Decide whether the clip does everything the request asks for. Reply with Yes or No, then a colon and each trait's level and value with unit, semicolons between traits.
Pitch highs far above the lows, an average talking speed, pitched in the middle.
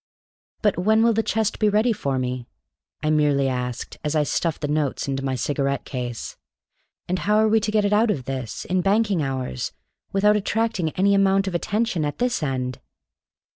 Yes: wide, 7.6 semitones; average, 190 wpm; medium, 175 Hz